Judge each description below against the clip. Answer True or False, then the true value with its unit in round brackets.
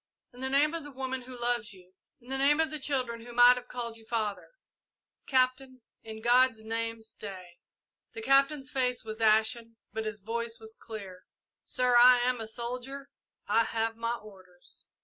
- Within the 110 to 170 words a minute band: False (180 wpm)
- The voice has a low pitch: False (235 Hz)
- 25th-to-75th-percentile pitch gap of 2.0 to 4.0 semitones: True (2.7 semitones)